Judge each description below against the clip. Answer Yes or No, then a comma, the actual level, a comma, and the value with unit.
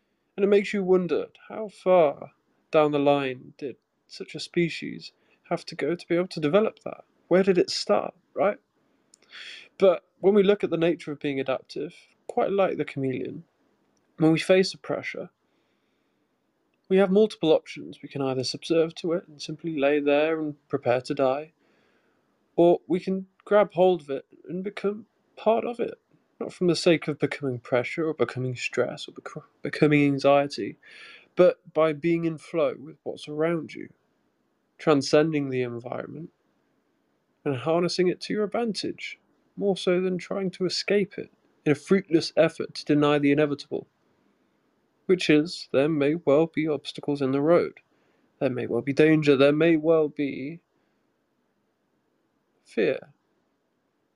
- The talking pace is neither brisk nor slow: Yes, average, 160 wpm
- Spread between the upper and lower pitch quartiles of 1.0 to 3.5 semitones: No, average, 4.2 semitones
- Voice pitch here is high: No, medium, 160 Hz